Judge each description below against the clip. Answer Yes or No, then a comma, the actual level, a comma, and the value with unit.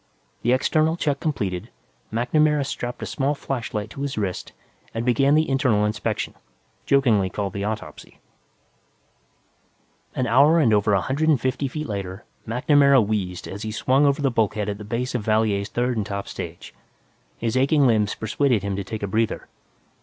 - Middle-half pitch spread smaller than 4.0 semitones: No, average, 4.9 semitones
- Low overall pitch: Yes, low, 115 Hz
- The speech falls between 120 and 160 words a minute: No, average, 170 wpm